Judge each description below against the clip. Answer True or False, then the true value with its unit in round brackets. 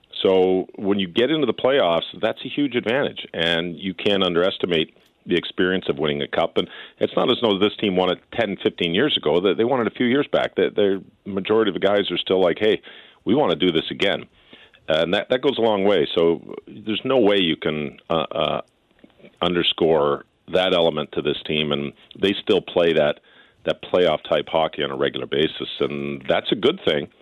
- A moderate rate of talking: False (215 wpm)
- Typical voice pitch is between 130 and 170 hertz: False (95 Hz)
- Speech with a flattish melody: False (3.6 semitones)